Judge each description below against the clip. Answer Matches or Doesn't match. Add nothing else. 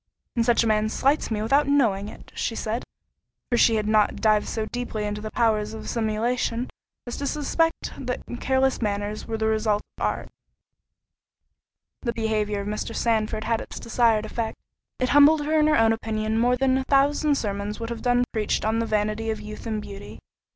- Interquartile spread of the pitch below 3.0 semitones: Matches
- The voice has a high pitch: Matches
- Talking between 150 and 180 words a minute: Doesn't match